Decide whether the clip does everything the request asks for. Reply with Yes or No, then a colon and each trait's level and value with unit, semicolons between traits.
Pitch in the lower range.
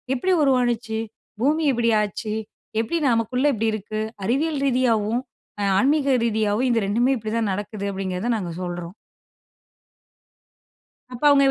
No: high, 230 Hz